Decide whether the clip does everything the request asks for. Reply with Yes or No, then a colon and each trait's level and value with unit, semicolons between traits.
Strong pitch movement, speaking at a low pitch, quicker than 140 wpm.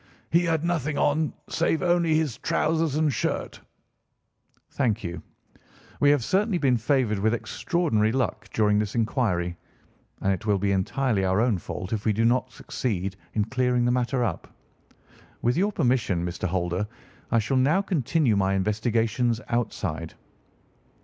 Yes: wide, 5.8 semitones; low, 120 Hz; average, 150 wpm